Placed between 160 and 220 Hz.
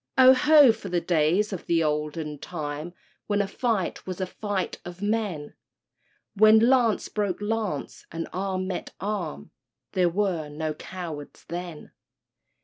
Yes: medium, 185 Hz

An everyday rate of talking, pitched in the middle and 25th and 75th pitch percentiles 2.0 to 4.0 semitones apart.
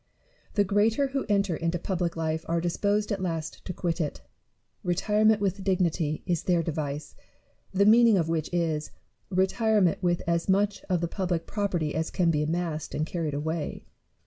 Yes: average, 170 wpm; medium, 175 Hz; average, 3.6 semitones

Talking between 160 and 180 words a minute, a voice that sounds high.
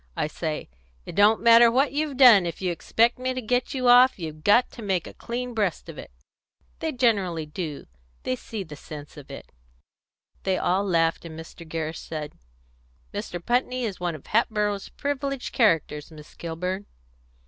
Yes: average, 175 wpm; high, 200 Hz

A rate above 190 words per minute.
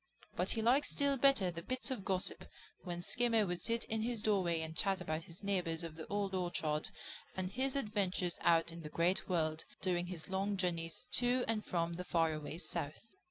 Yes: average, 200 wpm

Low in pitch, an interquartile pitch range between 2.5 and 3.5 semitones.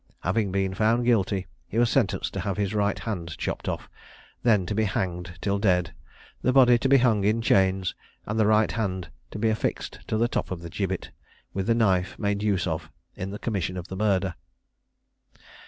Yes: low, 100 Hz; average, 2.9 semitones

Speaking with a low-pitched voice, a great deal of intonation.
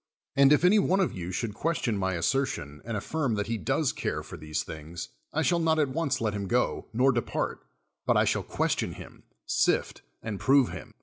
Yes: low, 115 Hz; wide, 7.7 semitones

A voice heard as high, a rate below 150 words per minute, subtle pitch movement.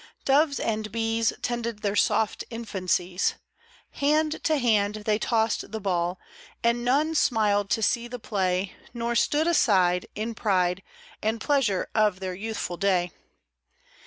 No: high, 220 Hz; slow, 135 wpm; average, 3.6 semitones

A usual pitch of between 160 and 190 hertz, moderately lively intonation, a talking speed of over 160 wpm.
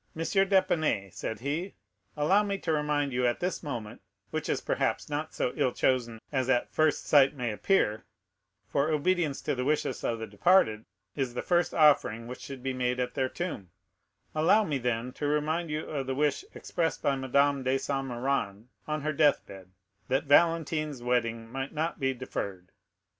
No: medium, 140 Hz; average, 4.0 semitones; average, 175 wpm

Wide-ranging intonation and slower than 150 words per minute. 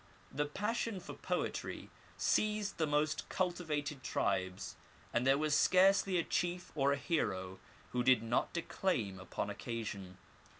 Yes: wide, 7.4 semitones; slow, 135 wpm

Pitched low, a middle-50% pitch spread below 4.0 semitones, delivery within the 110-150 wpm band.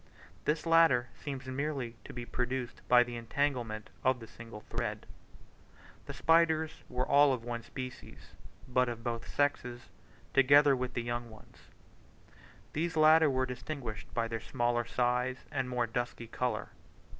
Yes: low, 125 Hz; average, 2.9 semitones; average, 145 wpm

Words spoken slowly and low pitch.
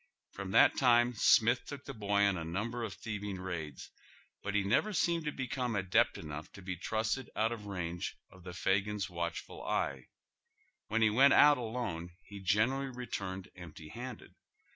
No: average, 180 wpm; low, 105 Hz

